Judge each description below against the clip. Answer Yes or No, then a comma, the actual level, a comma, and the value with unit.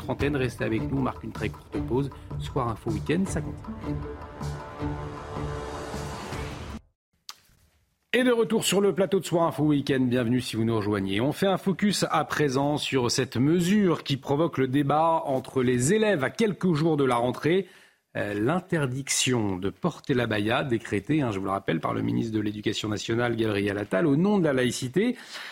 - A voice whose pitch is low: Yes, low, 125 Hz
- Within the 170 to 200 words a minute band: Yes, average, 180 wpm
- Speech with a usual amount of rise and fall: No, wide, 8.2 semitones